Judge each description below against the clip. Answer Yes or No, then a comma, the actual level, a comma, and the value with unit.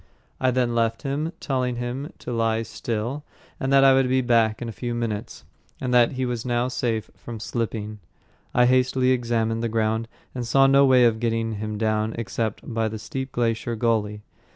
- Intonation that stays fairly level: Yes, narrow, 2.3 semitones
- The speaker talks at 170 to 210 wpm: Yes, average, 185 wpm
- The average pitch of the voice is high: No, low, 120 Hz